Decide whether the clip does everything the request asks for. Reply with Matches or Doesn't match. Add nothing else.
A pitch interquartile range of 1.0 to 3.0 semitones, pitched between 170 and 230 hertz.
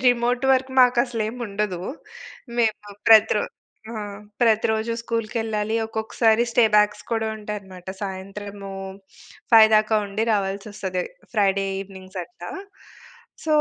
Matches